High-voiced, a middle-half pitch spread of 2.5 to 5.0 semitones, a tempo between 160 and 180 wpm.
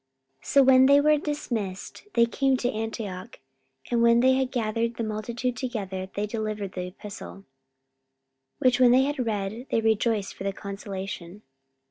Yes: high, 225 Hz; average, 4.0 semitones; average, 165 wpm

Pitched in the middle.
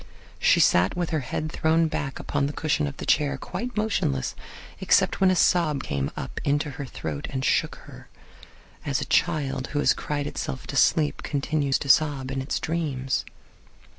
Yes: medium, 145 Hz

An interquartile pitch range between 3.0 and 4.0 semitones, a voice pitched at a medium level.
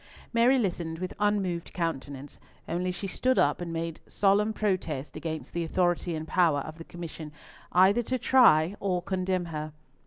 Yes: average, 3.3 semitones; medium, 175 Hz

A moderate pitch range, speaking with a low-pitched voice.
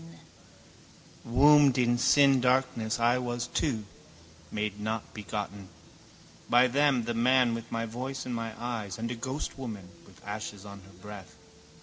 Yes: average, 3.2 semitones; low, 115 Hz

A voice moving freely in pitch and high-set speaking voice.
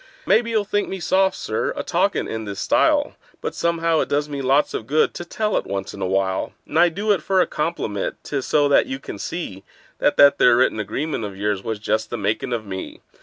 No: wide, 8.3 semitones; low, 135 Hz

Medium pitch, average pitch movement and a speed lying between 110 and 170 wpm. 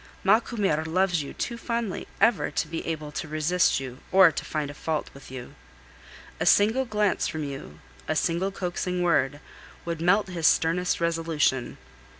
Yes: medium, 170 Hz; average, 4.1 semitones; average, 155 wpm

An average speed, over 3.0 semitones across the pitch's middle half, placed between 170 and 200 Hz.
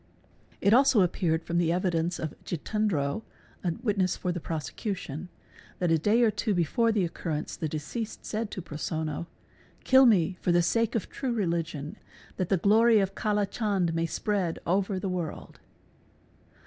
Yes: average, 170 wpm; average, 4.1 semitones; medium, 185 Hz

